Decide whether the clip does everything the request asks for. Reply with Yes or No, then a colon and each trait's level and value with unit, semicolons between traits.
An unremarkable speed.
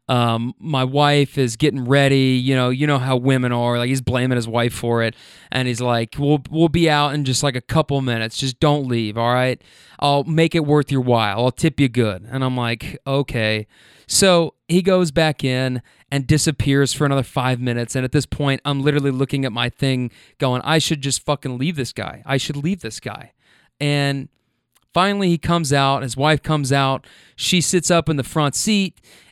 No: fast, 210 wpm